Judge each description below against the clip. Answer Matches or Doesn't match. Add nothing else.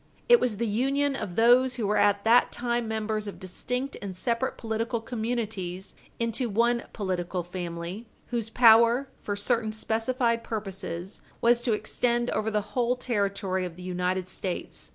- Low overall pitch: Doesn't match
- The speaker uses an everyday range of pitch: Matches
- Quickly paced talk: Doesn't match